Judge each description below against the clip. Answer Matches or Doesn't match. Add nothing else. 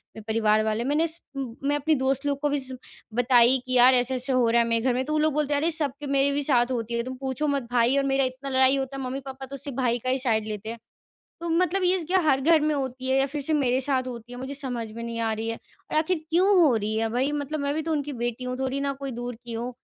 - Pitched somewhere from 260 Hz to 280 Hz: Matches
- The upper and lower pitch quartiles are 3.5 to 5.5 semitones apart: Doesn't match